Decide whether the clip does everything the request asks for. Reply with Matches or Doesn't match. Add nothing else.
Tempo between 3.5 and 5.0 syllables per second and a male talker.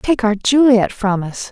Doesn't match